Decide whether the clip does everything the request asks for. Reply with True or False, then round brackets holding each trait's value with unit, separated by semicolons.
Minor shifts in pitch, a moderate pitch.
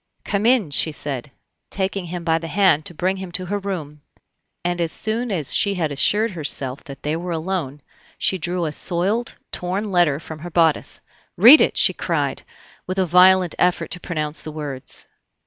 False (3.7 semitones; 175 Hz)